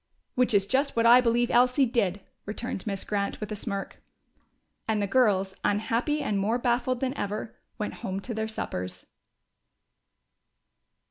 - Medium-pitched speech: No, high, 220 Hz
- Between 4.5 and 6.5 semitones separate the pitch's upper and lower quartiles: No, average, 3.7 semitones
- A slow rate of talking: No, average, 150 wpm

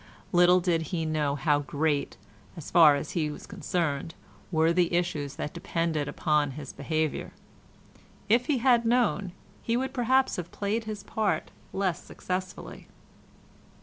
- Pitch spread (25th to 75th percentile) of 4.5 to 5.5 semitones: Yes, average, 5.0 semitones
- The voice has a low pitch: No, medium, 170 Hz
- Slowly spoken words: No, average, 145 wpm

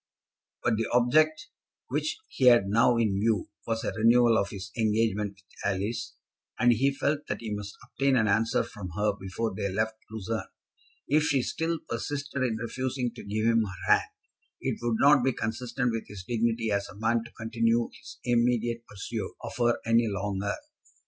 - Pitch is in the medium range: No, low, 115 Hz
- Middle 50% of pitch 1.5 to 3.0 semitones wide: Yes, narrow, 2.6 semitones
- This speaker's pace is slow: No, average, 180 wpm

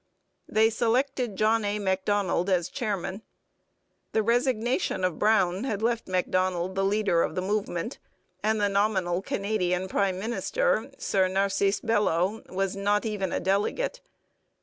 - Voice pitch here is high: Yes, high, 200 Hz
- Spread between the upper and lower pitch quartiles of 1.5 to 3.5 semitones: Yes, average, 2.8 semitones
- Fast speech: No, slow, 135 wpm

